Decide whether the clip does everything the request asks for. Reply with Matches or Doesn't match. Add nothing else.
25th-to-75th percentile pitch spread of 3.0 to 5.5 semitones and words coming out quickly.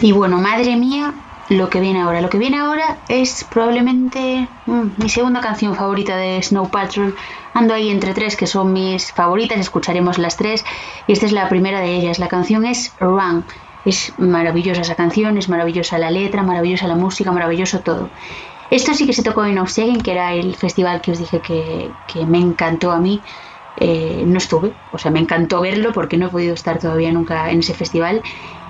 Matches